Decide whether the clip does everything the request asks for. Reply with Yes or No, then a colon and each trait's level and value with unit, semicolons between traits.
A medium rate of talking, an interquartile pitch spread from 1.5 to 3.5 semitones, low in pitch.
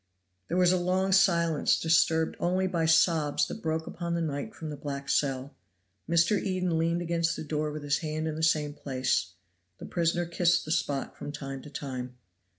No: average, 190 wpm; average, 2.8 semitones; medium, 160 Hz